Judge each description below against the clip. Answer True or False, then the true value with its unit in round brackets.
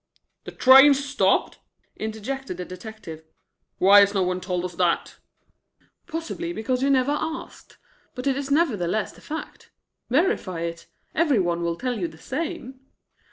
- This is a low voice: False (240 Hz)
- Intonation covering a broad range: True (7.5 semitones)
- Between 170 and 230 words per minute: False (150 wpm)